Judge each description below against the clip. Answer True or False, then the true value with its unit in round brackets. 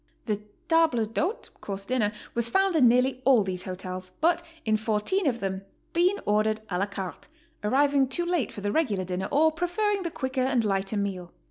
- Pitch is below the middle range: False (235 Hz)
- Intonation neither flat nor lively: False (7.9 semitones)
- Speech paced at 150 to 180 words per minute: False (190 wpm)